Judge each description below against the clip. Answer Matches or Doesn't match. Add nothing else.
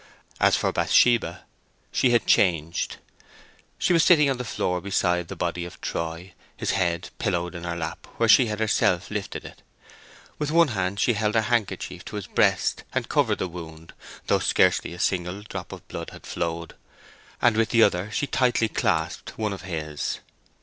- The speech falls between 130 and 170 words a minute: Doesn't match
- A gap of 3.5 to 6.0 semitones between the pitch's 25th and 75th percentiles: Matches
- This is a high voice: Doesn't match